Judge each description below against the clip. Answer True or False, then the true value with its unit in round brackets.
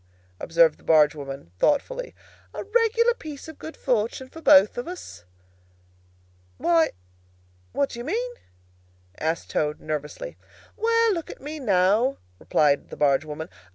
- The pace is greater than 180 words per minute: False (140 wpm)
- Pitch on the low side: False (240 Hz)